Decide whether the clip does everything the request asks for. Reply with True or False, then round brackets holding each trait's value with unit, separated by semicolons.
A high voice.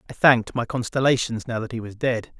False (120 Hz)